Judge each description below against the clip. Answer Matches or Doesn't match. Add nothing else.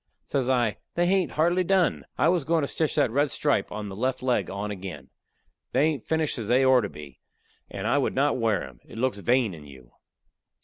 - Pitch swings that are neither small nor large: Doesn't match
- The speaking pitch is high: Doesn't match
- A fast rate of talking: Matches